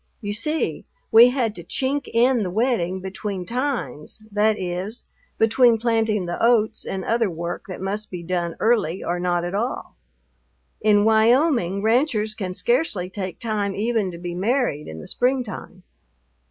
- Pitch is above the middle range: Yes, high, 210 Hz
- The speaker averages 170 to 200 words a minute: No, average, 155 wpm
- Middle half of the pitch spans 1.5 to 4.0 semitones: No, average, 4.5 semitones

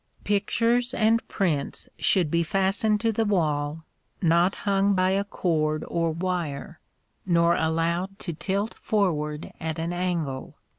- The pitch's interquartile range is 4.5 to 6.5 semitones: No, average, 3.7 semitones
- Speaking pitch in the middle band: Yes, medium, 175 Hz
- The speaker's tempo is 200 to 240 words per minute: No, slow, 135 wpm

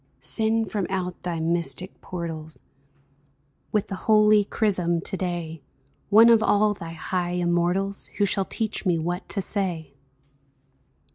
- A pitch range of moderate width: Yes, average, 3.2 semitones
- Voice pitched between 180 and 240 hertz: Yes, medium, 185 Hz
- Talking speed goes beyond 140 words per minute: No, slow, 135 wpm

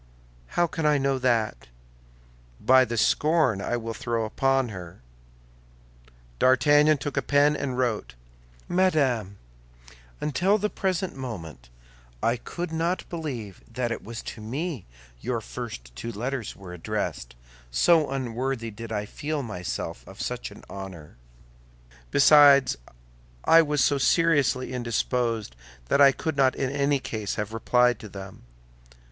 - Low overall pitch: Yes, low, 130 Hz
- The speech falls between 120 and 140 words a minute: Yes, slow, 135 wpm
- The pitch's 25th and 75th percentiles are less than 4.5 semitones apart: No, average, 5.1 semitones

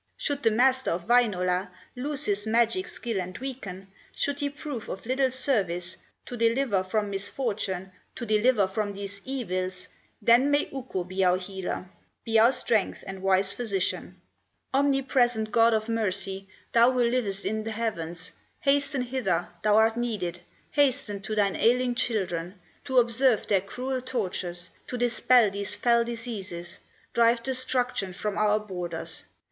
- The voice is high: Yes, high, 220 Hz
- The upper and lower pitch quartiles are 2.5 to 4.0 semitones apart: No, average, 4.5 semitones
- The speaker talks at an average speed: Yes, average, 150 wpm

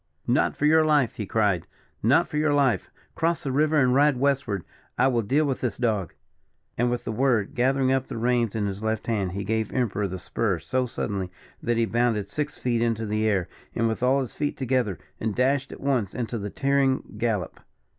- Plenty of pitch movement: No, average, 4.0 semitones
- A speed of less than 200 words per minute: No, fast, 205 wpm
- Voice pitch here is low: Yes, low, 120 Hz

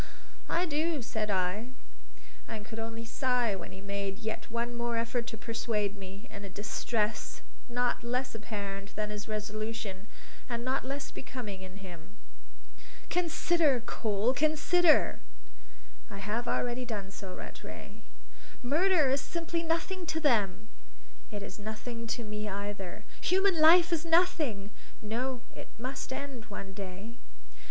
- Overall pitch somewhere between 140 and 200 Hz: No, high, 230 Hz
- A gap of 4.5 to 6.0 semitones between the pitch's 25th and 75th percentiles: Yes, average, 4.8 semitones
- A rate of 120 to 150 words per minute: Yes, average, 140 wpm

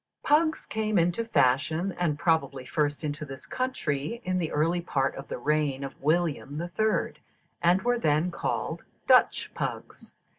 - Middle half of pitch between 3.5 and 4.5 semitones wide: Yes, average, 4.1 semitones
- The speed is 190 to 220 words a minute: No, average, 160 wpm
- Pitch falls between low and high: Yes, medium, 160 Hz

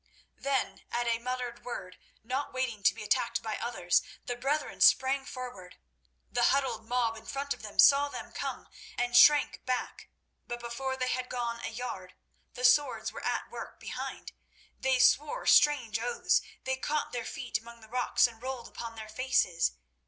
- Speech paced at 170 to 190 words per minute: Yes, average, 175 wpm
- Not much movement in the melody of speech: Yes, narrow, 2.3 semitones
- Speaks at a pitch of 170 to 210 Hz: No, high, 245 Hz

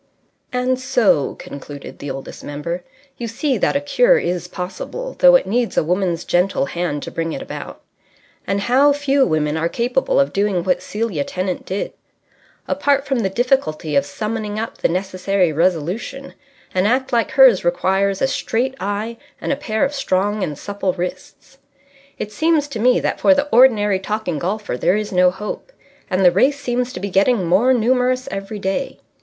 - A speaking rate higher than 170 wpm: Yes, average, 180 wpm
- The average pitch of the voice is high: Yes, high, 205 Hz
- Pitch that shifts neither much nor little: No, wide, 6.0 semitones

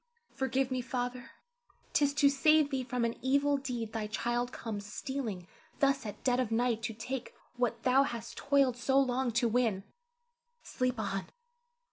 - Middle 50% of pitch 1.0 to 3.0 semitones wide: Yes, average, 2.7 semitones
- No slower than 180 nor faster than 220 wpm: No, average, 160 wpm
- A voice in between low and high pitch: No, very high, 250 Hz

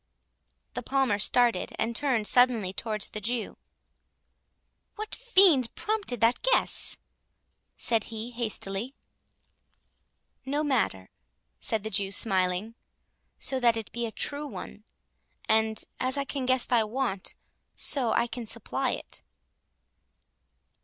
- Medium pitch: No, high, 235 Hz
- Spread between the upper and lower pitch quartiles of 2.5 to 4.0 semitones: Yes, average, 3.5 semitones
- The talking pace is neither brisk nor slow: No, slow, 115 wpm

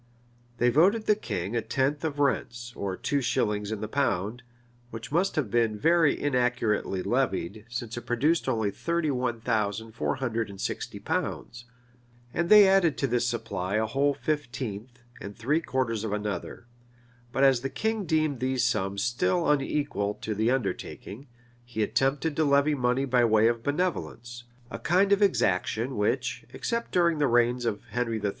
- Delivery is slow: No, average, 170 wpm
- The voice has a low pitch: Yes, low, 120 Hz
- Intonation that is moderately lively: Yes, average, 4.6 semitones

